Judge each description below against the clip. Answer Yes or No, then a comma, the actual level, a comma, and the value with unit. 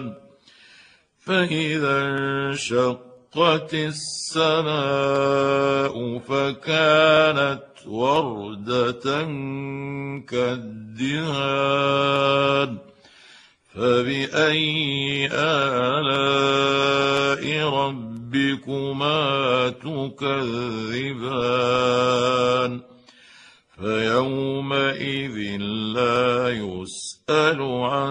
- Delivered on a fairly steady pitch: Yes, narrow, 2.0 semitones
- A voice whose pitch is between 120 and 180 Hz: Yes, medium, 140 Hz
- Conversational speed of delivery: No, slow, 30 wpm